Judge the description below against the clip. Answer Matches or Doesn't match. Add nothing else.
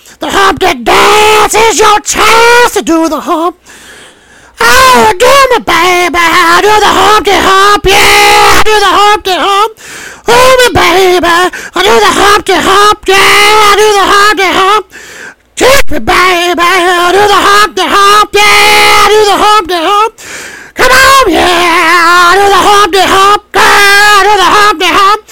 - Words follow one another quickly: Doesn't match